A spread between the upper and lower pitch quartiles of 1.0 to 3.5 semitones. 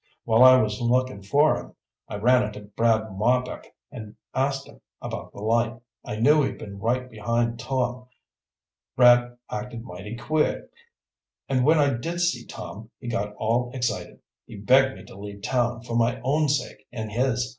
Yes: average, 2.7 semitones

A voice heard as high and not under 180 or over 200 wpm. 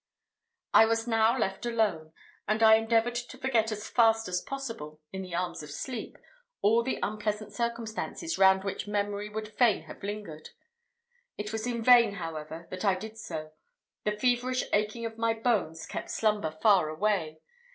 No: high, 215 Hz; average, 165 wpm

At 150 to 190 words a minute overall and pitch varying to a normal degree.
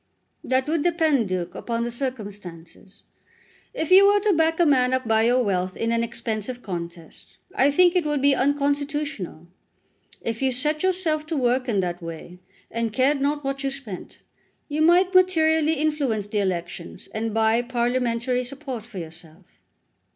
No: average, 165 wpm; wide, 5.9 semitones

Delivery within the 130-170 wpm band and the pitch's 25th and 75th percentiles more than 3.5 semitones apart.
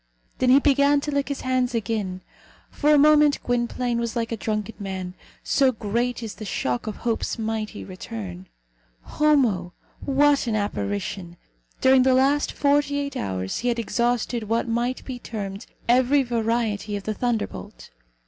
Yes: average, 160 wpm; average, 4.2 semitones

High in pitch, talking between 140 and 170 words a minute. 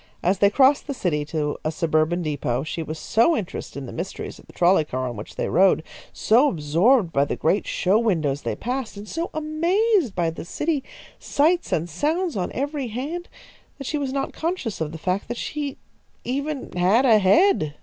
No: high, 210 Hz; average, 200 wpm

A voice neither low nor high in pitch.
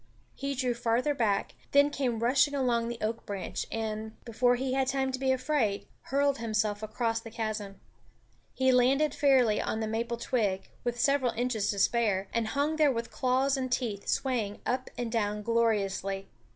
No: high, 235 Hz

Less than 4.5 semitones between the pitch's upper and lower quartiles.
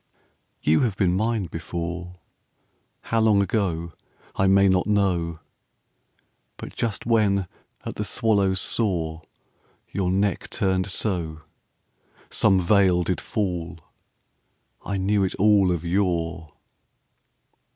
Yes: average, 2.8 semitones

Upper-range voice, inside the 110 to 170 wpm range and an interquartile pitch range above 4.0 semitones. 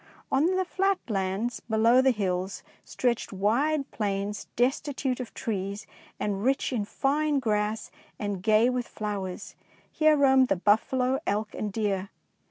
Yes: high, 225 Hz; average, 140 wpm; average, 4.7 semitones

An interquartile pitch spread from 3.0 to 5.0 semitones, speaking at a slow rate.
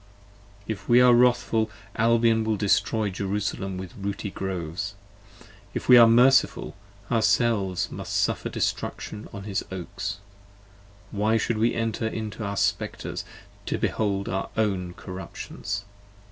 No: narrow, 2.6 semitones; slow, 125 wpm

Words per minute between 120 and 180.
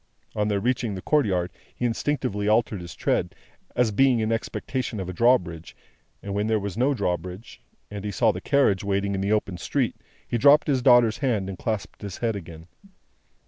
No: average, 190 wpm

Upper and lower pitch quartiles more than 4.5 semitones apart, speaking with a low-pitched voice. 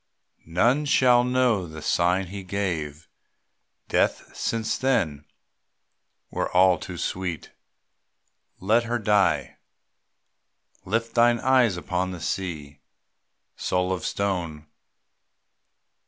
Yes: average, 4.9 semitones; very low, 95 Hz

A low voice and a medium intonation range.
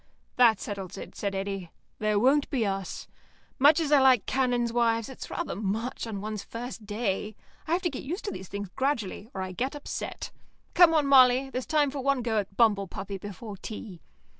No: high, 230 Hz; average, 4.8 semitones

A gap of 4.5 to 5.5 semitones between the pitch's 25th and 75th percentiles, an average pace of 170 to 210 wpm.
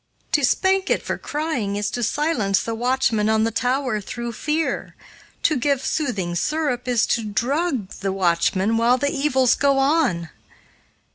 No: average, 5.1 semitones; average, 155 wpm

